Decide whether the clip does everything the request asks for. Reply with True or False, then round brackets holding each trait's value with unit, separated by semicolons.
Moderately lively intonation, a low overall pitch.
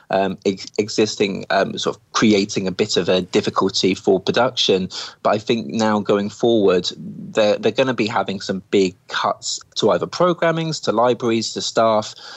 True (3.7 semitones; 110 Hz)